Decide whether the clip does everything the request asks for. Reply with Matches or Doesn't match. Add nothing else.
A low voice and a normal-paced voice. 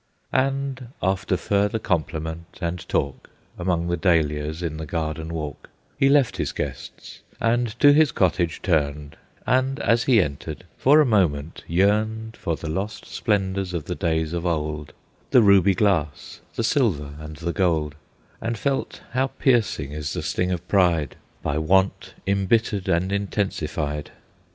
Matches